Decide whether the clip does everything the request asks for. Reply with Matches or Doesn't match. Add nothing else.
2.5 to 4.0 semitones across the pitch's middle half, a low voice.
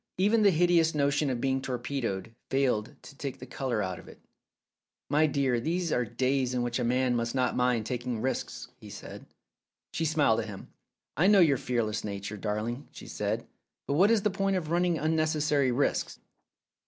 Doesn't match